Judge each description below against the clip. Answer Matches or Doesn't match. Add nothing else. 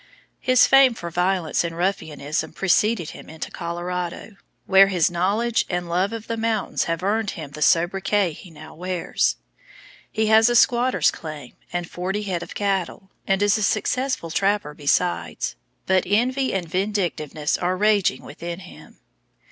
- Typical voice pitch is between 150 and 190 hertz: Matches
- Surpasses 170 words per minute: Doesn't match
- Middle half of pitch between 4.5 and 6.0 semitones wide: Doesn't match